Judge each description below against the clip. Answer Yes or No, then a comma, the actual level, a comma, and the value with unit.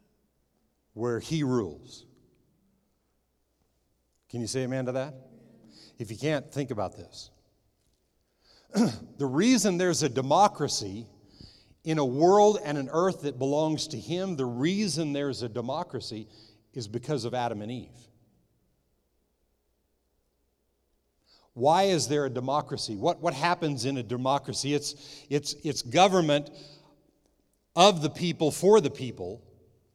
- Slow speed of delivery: Yes, slow, 125 wpm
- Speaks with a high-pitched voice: No, low, 130 Hz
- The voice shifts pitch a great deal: Yes, wide, 6.0 semitones